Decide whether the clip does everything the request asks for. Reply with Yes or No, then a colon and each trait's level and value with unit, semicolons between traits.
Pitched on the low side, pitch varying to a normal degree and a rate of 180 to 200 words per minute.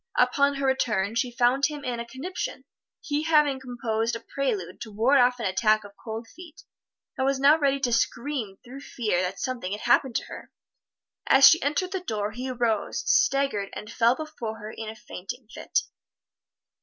No: high, 245 Hz; average, 4.0 semitones; average, 185 wpm